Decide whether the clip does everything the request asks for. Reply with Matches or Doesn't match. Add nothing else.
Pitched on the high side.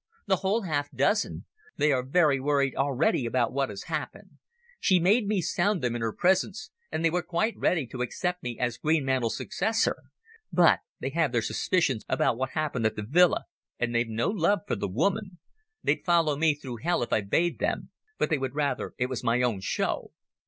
Doesn't match